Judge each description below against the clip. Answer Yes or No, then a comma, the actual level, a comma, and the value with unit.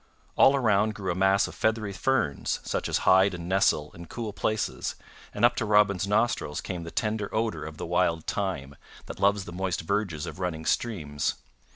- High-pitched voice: No, very low, 95 Hz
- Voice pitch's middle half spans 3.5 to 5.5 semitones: Yes, average, 4.0 semitones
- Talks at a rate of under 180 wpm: No, average, 190 wpm